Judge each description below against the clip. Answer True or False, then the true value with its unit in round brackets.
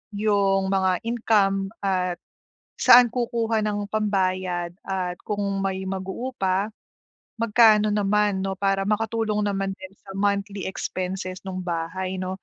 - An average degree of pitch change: False (1.9 semitones)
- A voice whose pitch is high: True (195 Hz)